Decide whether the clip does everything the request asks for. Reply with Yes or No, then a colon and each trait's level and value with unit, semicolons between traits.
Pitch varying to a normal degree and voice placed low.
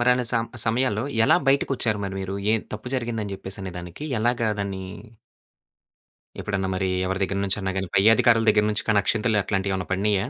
Yes: average, 3.0 semitones; low, 105 Hz